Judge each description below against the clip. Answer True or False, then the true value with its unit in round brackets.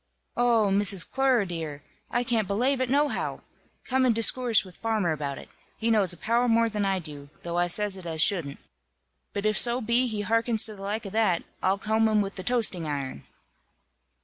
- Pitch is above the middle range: True (210 Hz)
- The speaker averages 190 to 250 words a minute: True (200 wpm)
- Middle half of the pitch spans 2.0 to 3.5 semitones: False (4.3 semitones)